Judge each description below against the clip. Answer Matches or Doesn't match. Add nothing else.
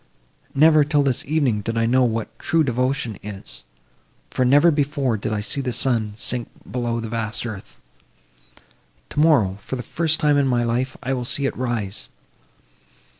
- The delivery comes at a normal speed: Matches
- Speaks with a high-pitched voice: Doesn't match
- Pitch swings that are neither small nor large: Matches